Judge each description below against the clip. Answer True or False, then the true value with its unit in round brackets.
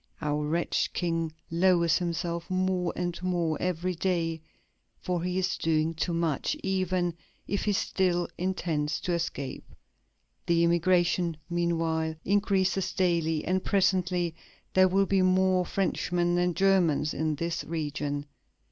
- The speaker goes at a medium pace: False (130 wpm)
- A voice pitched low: False (175 Hz)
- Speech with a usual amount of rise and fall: False (2.0 semitones)